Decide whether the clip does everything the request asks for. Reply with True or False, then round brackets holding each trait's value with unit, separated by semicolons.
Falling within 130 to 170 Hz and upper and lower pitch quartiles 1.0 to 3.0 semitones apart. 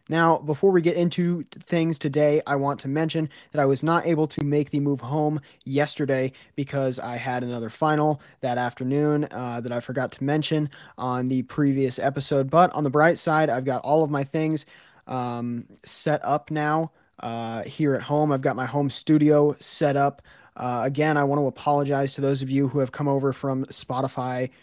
True (140 Hz; 2.6 semitones)